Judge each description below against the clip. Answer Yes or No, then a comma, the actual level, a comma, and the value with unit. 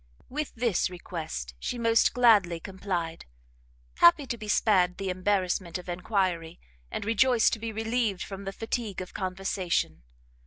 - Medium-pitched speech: No, high, 195 Hz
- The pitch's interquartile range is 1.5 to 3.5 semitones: No, average, 3.9 semitones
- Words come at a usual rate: Yes, average, 145 wpm